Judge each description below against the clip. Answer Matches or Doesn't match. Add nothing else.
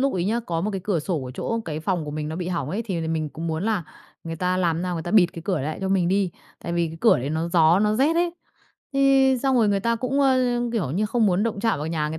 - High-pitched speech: Doesn't match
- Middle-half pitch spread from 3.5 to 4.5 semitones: Doesn't match